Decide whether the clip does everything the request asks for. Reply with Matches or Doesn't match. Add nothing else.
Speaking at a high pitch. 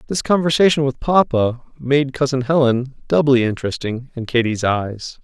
Doesn't match